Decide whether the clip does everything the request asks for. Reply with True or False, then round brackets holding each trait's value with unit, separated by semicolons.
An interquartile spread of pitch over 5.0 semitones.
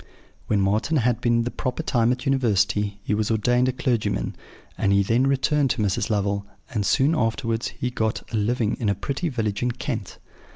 False (3.5 semitones)